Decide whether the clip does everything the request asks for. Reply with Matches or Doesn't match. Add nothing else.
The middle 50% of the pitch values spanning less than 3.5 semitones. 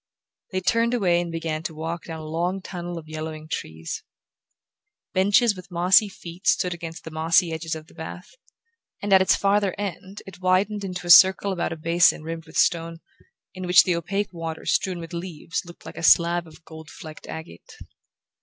Matches